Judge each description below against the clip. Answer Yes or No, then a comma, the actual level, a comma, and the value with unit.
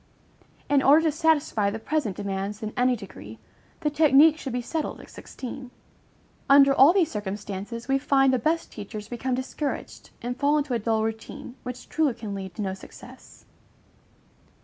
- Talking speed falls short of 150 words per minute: No, average, 170 wpm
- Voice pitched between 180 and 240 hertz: No, very high, 250 Hz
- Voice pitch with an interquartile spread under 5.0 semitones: No, average, 5.3 semitones